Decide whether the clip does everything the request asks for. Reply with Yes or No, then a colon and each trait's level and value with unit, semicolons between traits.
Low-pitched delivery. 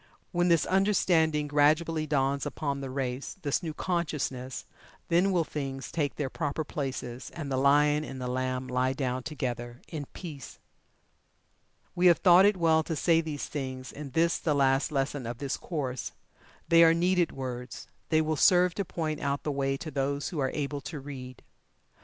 No: medium, 145 Hz